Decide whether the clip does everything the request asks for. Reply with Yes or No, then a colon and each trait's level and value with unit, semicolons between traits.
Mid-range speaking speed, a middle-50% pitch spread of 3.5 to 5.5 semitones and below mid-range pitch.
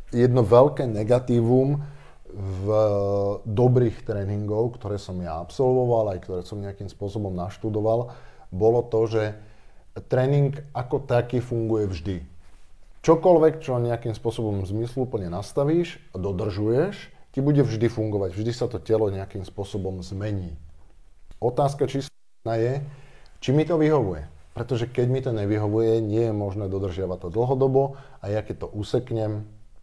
Yes: average, 135 wpm; average, 3.9 semitones; low, 110 Hz